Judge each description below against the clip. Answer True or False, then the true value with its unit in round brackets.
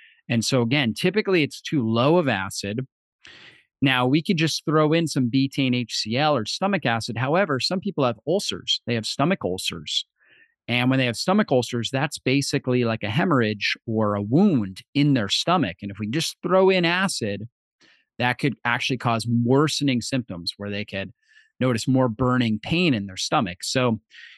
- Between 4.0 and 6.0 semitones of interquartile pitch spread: True (5.0 semitones)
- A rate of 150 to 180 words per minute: True (175 wpm)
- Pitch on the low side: True (130 Hz)